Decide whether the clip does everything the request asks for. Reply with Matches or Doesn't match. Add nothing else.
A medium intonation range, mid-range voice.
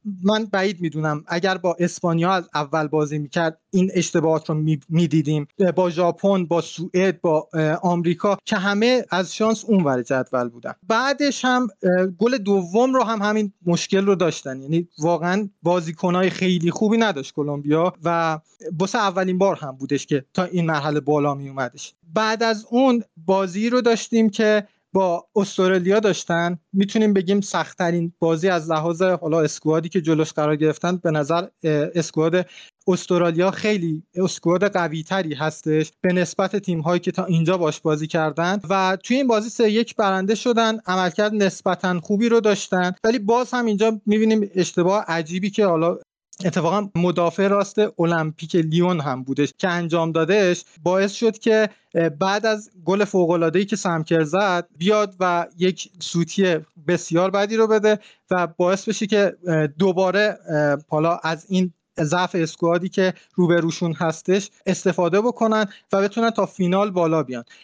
Matches